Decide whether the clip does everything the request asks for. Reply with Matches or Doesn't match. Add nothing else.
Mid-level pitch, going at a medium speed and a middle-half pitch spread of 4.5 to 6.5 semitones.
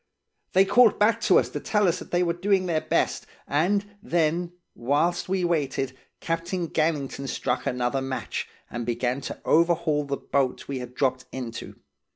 Matches